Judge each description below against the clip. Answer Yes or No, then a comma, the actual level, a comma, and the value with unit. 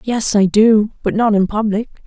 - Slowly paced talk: No, fast, 205 wpm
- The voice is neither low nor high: No, high, 215 Hz